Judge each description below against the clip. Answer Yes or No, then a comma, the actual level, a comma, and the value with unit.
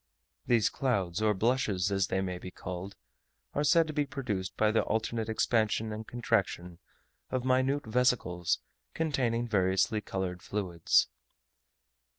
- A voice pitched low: Yes, low, 110 Hz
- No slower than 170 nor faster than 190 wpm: No, slow, 135 wpm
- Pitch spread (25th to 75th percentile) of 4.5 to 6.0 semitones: Yes, average, 4.9 semitones